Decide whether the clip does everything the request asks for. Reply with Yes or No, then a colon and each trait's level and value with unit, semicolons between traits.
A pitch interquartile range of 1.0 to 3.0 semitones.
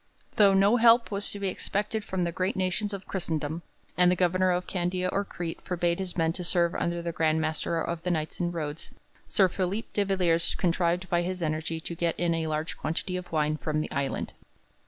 Yes: narrow, 2.4 semitones